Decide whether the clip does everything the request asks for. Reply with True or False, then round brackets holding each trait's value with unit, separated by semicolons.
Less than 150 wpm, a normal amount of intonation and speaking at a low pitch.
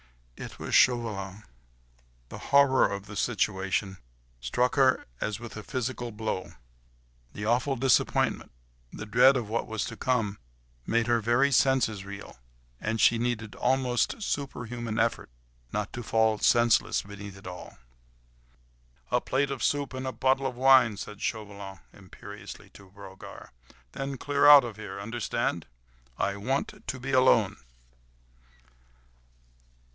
True (135 wpm; 4.1 semitones; 115 Hz)